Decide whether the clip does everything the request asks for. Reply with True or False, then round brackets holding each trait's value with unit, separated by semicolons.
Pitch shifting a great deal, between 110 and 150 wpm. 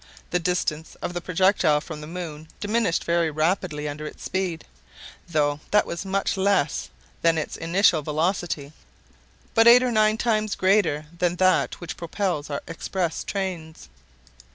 False (3.8 semitones; 145 wpm)